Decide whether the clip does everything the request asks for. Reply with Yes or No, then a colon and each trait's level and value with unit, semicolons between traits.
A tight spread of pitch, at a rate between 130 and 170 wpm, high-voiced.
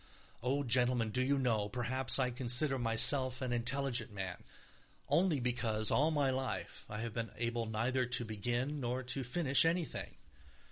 No: narrow, 2.3 semitones; average, 155 wpm; low, 125 Hz